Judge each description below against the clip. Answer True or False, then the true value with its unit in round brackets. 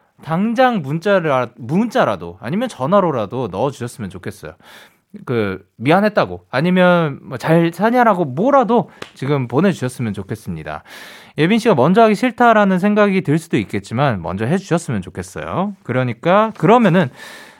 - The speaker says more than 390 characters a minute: False (340 characters per minute)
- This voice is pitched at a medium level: True (160 Hz)